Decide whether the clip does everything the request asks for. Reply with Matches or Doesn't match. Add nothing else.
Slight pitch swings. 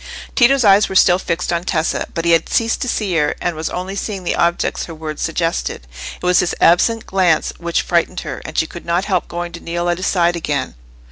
Matches